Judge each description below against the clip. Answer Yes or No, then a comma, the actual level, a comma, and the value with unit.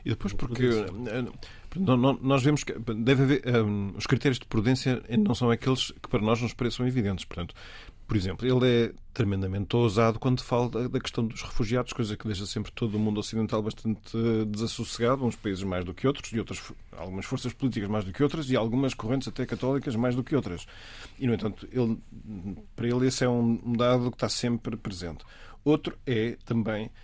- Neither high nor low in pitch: No, low, 115 Hz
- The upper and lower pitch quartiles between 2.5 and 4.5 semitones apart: Yes, average, 2.8 semitones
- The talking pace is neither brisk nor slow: No, fast, 190 wpm